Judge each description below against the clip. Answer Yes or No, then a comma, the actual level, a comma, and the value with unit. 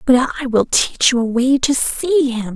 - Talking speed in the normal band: No, fast, 235 wpm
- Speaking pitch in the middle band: No, very high, 255 Hz